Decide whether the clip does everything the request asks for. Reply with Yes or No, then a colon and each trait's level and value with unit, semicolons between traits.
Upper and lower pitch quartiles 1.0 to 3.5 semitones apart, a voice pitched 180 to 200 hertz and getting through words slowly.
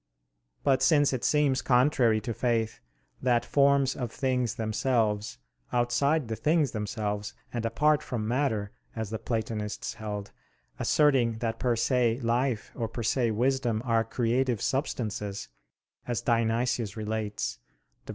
No: average, 2.9 semitones; low, 120 Hz; slow, 130 wpm